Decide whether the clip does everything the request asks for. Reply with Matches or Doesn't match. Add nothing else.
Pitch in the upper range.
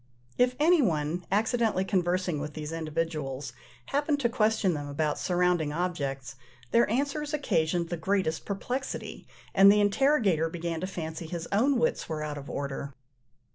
Doesn't match